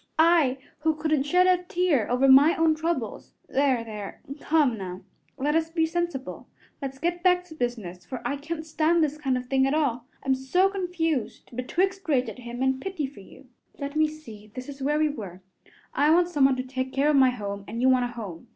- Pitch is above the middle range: Yes, very high, 280 Hz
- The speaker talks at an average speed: No, fast, 215 wpm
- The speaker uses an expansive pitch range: No, average, 4.3 semitones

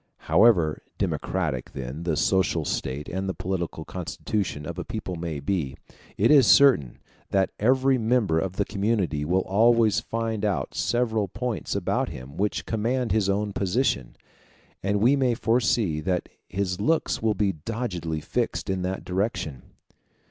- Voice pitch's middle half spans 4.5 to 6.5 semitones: Yes, average, 4.9 semitones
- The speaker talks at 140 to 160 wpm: Yes, average, 150 wpm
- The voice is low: Yes, low, 100 Hz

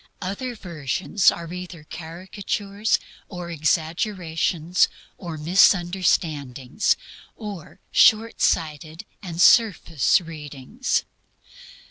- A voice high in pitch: No, medium, 175 Hz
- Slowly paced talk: Yes, slow, 70 wpm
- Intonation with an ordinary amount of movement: Yes, average, 3.7 semitones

